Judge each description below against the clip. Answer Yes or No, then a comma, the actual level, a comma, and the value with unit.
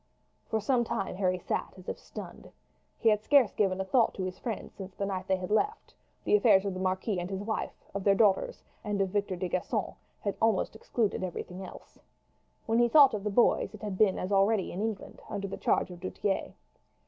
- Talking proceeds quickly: Yes, fast, 220 wpm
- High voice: Yes, high, 200 Hz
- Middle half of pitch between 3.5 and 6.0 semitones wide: No, average, 2.8 semitones